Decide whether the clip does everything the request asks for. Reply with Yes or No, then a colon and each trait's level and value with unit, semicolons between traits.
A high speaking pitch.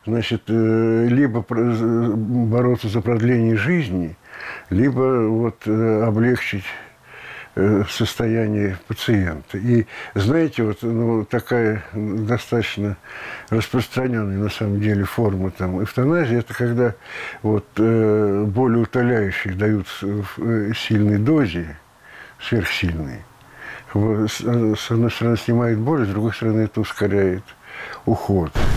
No: low, 110 Hz